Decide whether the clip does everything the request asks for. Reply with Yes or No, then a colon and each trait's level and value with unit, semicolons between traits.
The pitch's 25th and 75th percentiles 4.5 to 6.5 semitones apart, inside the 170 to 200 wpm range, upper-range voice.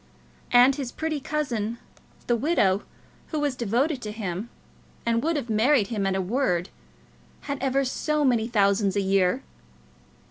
No: wide, 5.6 semitones; average, 150 wpm; high, 235 Hz